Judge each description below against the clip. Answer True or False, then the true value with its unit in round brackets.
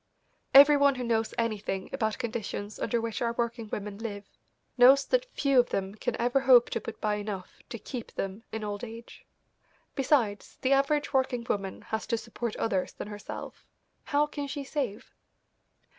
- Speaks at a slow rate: False (175 wpm)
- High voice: True (235 Hz)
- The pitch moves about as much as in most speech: True (4.1 semitones)